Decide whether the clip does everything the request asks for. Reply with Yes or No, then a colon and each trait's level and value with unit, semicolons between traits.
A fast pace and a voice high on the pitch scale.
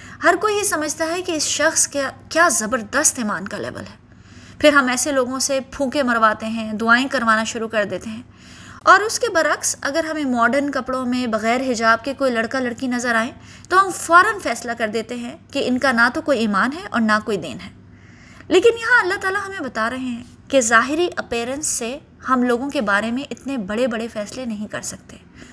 Yes: fast, 210 wpm; very high, 255 Hz